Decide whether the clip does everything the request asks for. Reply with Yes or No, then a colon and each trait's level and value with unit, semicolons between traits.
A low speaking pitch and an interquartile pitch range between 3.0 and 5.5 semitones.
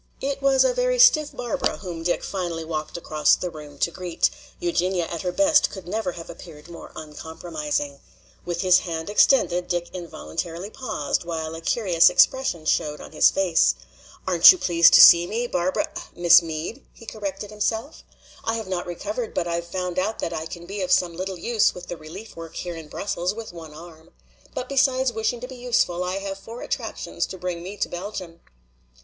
No: medium, 180 Hz; average, 4.6 semitones